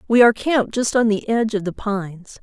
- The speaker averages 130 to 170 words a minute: No, fast, 245 wpm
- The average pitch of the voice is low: No, high, 215 Hz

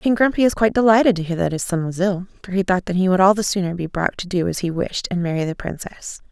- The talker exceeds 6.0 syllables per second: Yes, 6.5 syllables/s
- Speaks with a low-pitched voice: No, high, 190 Hz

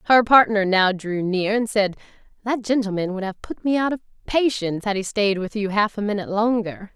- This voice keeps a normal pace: No, fast, 215 wpm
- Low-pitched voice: No, high, 210 Hz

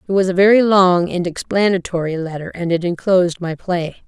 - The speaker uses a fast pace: No, average, 190 wpm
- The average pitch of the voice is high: No, medium, 180 Hz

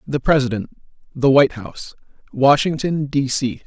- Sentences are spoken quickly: No, slow, 130 wpm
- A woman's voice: No, male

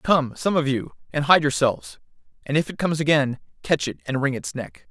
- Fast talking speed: Yes, fast, 220 wpm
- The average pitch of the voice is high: No, medium, 145 Hz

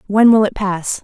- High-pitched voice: Yes, high, 200 Hz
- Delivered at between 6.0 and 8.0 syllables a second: No, 4.6 syllables/s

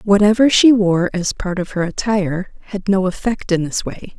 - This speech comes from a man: No, female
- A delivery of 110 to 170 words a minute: No, average, 200 wpm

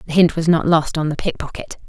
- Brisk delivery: Yes, fast, 285 wpm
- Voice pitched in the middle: Yes, medium, 160 Hz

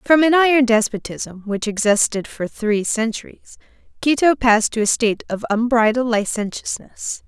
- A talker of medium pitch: No, high, 230 Hz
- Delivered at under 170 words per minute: Yes, average, 140 wpm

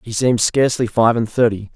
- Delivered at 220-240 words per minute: No, fast, 205 wpm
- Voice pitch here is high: No, low, 115 Hz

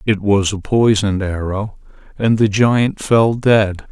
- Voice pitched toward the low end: Yes, low, 105 Hz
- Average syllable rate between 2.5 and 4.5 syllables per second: Yes, 3.8 syllables/s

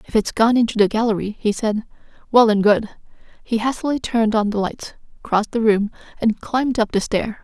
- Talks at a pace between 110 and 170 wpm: No, average, 200 wpm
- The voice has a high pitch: Yes, high, 220 Hz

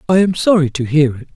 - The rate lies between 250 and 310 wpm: Yes, fast, 265 wpm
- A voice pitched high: No, medium, 155 Hz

